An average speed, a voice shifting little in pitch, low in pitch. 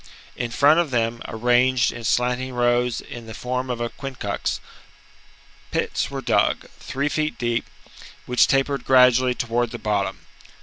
Yes: average, 150 wpm; narrow, 1.8 semitones; low, 125 Hz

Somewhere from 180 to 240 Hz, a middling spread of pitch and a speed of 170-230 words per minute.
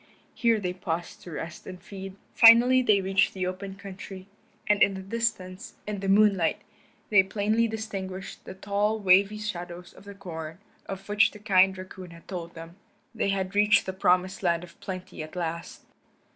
No: high, 190 Hz; narrow, 2.2 semitones; average, 175 wpm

